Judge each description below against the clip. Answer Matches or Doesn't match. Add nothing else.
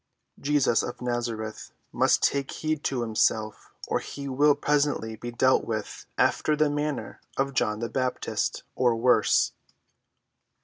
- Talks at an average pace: Doesn't match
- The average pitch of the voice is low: Matches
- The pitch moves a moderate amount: Matches